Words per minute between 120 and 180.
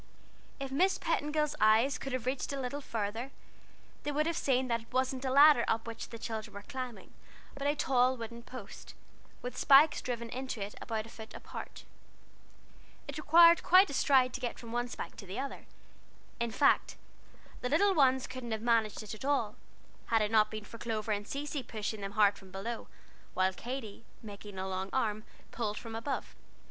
No: average, 190 wpm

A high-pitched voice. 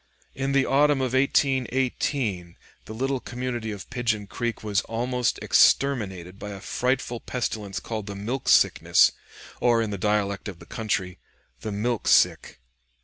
No: low, 115 Hz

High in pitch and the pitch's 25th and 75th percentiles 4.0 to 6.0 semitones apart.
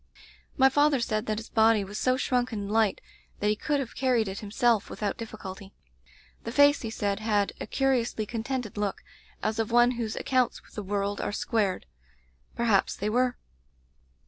No: high, 225 Hz; average, 3.2 semitones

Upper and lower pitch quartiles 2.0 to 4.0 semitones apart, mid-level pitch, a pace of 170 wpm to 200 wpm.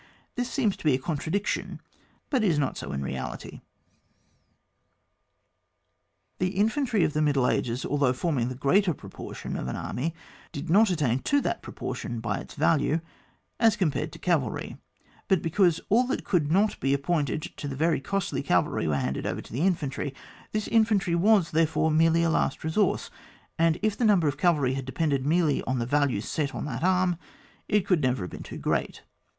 No: wide, 5.5 semitones; medium, 160 Hz; average, 185 wpm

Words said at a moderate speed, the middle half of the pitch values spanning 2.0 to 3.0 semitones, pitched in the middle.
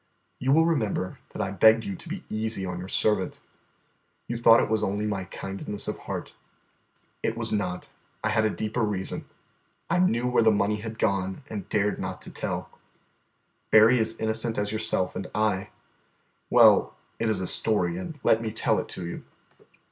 No: average, 185 wpm; narrow, 2.4 semitones; low, 110 Hz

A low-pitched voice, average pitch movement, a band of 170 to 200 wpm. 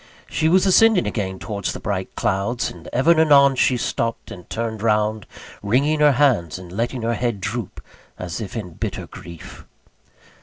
No: low, 115 Hz; wide, 5.9 semitones; average, 175 wpm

